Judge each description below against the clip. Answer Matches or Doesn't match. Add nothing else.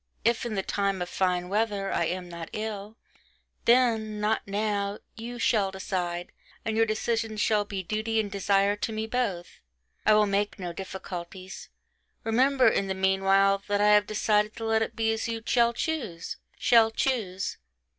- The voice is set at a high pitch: Matches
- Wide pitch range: Doesn't match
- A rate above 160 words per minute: Matches